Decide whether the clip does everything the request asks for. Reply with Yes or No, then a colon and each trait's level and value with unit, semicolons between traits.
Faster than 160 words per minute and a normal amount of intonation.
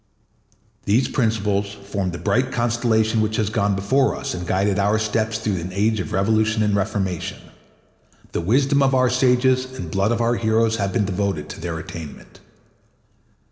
Yes: average, 170 wpm; average, 3.2 semitones